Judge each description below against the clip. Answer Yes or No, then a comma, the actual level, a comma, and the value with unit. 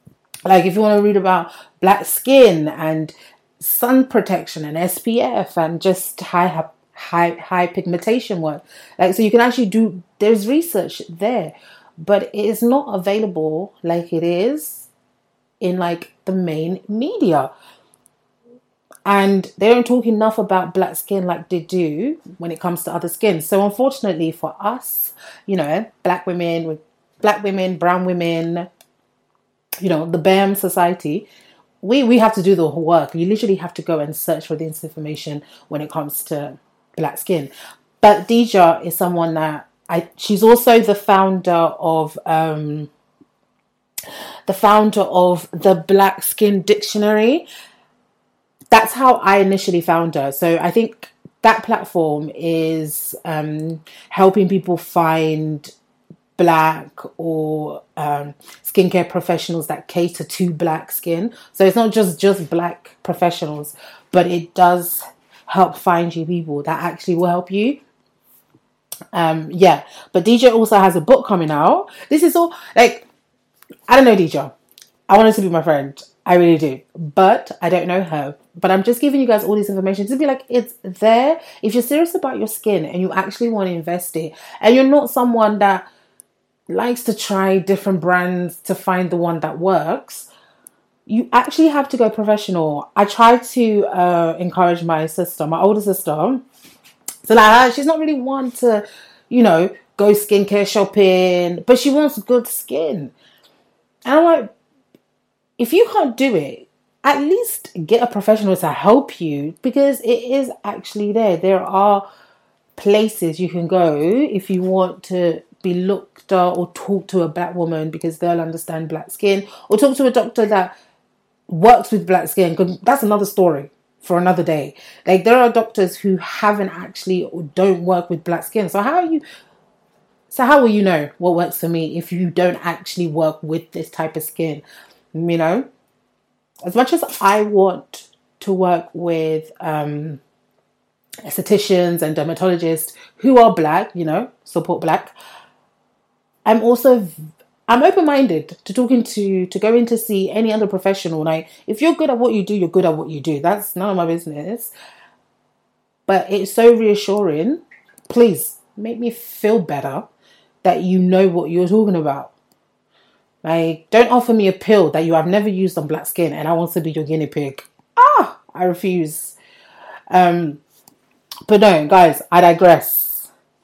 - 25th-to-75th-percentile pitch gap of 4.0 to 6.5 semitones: Yes, average, 4.4 semitones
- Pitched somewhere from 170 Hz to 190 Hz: Yes, medium, 185 Hz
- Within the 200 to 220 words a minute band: No, average, 165 wpm